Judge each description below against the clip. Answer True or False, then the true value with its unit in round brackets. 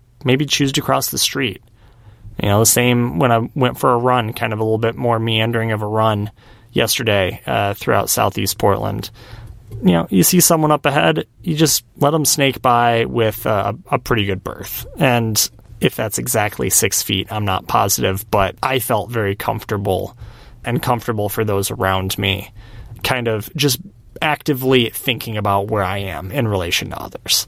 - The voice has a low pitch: True (115 Hz)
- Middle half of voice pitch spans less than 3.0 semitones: False (3.7 semitones)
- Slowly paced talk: False (180 wpm)